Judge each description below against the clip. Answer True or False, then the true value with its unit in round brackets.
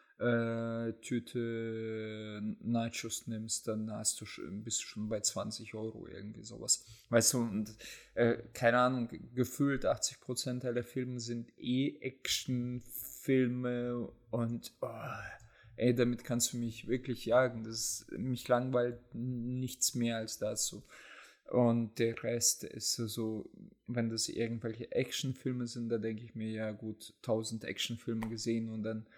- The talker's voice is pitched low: True (115 Hz)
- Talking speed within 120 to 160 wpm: True (140 wpm)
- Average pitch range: False (1.6 semitones)